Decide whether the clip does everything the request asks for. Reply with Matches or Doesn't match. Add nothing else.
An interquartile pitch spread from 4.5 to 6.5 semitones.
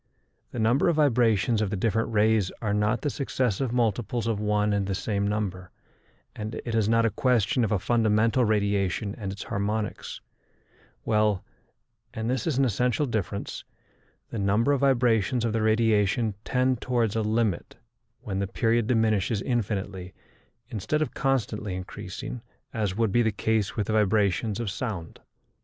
Doesn't match